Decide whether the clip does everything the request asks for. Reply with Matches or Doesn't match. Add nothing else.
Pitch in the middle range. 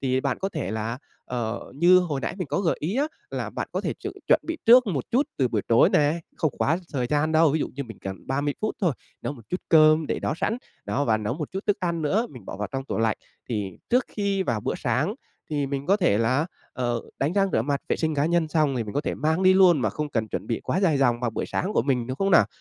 Matches